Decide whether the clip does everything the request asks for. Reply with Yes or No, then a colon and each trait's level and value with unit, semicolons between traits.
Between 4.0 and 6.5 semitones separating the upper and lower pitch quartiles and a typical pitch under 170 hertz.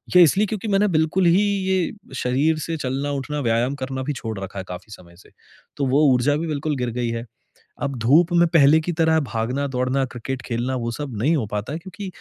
Yes: average, 4.7 semitones; medium, 140 Hz